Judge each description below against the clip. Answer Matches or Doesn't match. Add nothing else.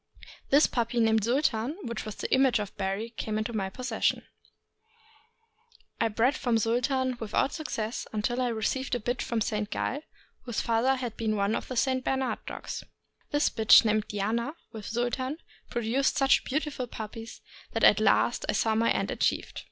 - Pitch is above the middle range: Matches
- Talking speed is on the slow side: Doesn't match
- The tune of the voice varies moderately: Matches